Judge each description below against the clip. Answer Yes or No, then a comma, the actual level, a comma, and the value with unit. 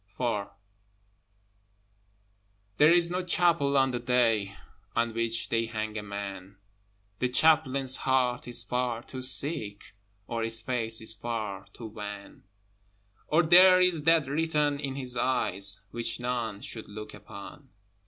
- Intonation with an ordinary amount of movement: Yes, average, 4.5 semitones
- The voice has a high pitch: No, low, 120 Hz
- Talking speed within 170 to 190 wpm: No, slow, 135 wpm